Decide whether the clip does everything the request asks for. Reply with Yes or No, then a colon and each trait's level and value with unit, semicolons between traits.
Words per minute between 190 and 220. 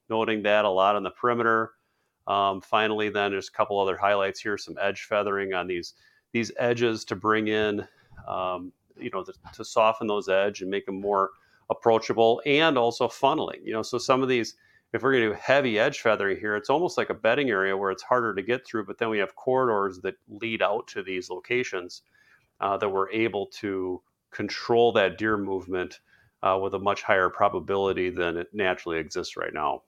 Yes: fast, 205 wpm